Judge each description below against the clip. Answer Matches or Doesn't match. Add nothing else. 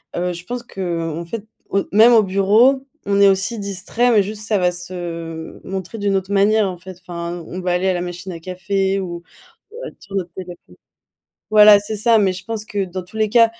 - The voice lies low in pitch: Doesn't match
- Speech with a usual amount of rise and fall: Matches